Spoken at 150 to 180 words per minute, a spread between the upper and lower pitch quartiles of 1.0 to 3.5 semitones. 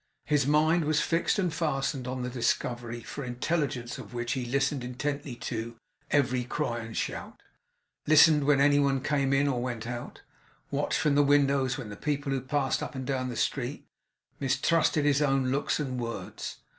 Yes: average, 175 wpm; average, 2.9 semitones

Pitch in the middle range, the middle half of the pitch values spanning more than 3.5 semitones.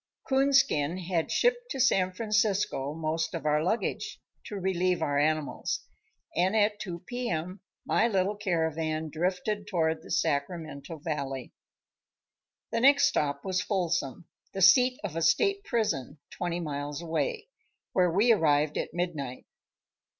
Yes: medium, 175 Hz; average, 5.0 semitones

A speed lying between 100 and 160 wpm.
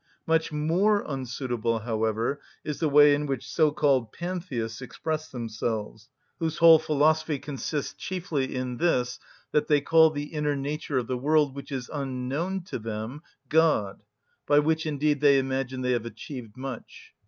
Yes: average, 155 wpm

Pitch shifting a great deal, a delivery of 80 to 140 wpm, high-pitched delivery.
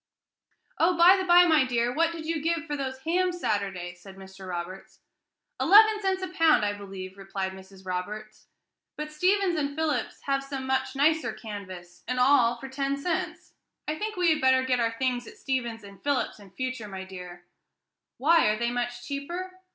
No: wide, 8.0 semitones; average, 185 wpm; very high, 260 Hz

